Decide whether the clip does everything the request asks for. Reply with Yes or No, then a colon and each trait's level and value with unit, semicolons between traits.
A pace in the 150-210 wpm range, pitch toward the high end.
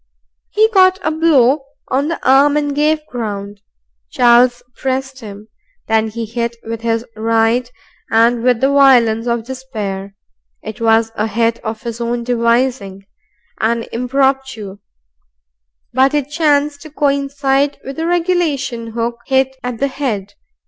No: average, 140 wpm; high, 245 Hz